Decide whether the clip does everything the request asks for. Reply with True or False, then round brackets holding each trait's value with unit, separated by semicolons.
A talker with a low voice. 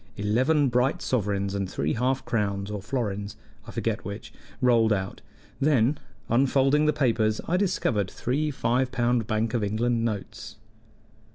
True (115 Hz)